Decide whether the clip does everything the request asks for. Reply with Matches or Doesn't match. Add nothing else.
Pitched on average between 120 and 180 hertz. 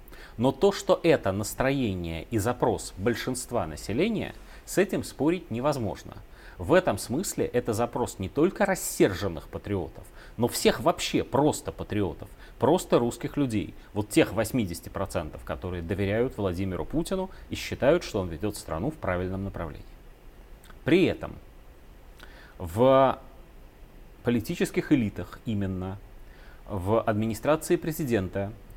Doesn't match